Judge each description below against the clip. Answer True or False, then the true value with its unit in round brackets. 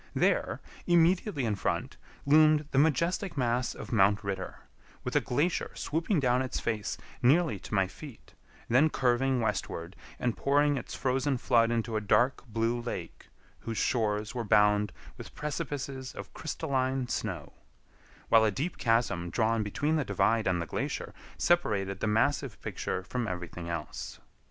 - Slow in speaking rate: False (150 wpm)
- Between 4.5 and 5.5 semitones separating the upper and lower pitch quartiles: True (5.0 semitones)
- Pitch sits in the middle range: False (120 Hz)